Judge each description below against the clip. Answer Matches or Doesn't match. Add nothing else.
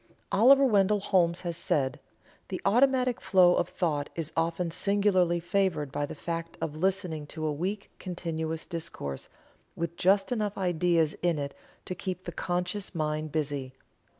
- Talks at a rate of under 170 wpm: Matches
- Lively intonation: Doesn't match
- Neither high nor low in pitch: Matches